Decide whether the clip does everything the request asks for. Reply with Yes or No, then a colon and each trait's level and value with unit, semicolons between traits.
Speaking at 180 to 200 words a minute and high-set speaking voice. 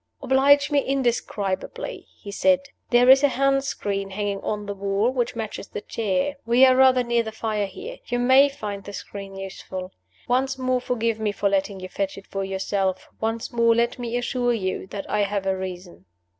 Yes: average, 195 wpm; high, 225 Hz